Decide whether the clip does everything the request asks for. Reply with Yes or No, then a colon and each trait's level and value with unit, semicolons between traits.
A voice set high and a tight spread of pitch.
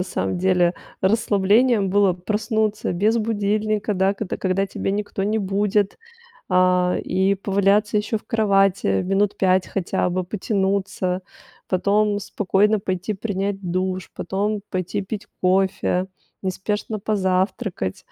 Yes: high, 195 Hz; narrow, 2.1 semitones